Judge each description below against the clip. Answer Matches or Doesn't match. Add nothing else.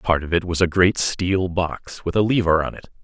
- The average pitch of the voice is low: Matches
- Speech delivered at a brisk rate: Matches